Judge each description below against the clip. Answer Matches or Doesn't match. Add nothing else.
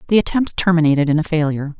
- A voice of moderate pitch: Matches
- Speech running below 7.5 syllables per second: Doesn't match